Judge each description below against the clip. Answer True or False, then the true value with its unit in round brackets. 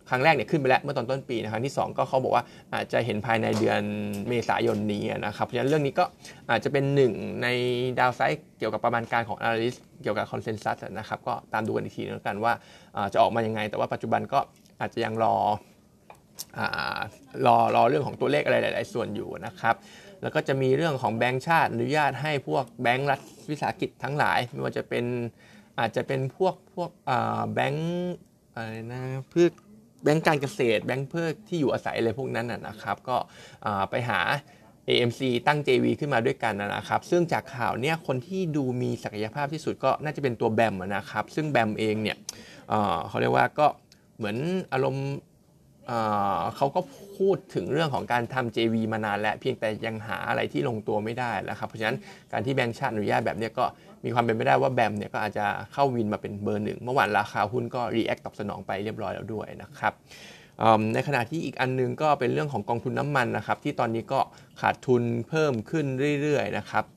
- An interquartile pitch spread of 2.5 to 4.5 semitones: True (4.0 semitones)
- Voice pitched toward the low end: True (125 Hz)